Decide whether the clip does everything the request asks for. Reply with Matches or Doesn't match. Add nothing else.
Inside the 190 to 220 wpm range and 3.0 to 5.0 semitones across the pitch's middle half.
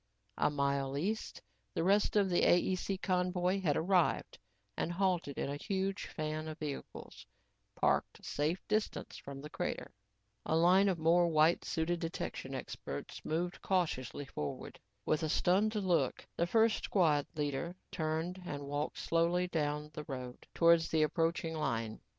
Doesn't match